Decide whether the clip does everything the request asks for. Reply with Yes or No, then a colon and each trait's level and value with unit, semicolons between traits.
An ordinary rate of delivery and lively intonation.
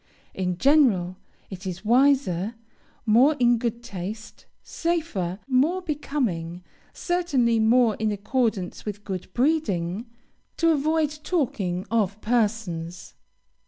No: slow, 105 wpm; wide, 6.9 semitones